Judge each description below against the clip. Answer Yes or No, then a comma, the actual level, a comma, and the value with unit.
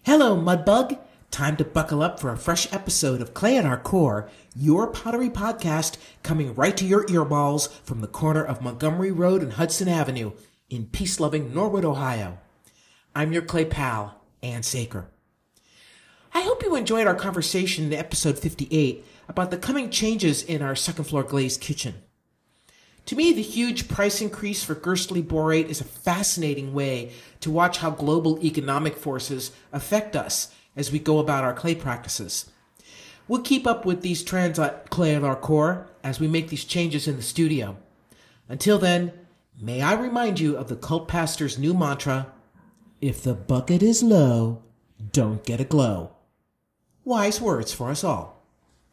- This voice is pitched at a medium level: Yes, medium, 155 Hz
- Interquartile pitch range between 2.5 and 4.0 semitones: No, average, 5.3 semitones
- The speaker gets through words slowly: No, average, 165 wpm